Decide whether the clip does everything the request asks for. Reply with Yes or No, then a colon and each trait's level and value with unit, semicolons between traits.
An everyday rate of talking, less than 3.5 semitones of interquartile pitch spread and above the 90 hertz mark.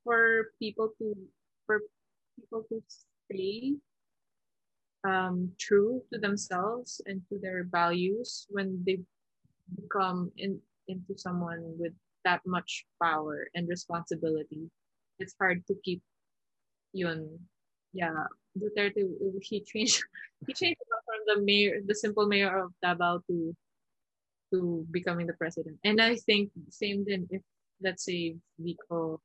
Yes: average, 125 wpm; average, 3.1 semitones; high, 190 Hz